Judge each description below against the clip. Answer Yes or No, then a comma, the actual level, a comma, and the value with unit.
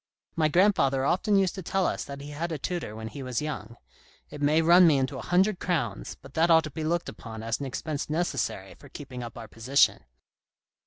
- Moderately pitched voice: Yes, medium, 150 Hz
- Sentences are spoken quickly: Yes, fast, 220 wpm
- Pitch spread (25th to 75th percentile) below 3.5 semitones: No, average, 4.6 semitones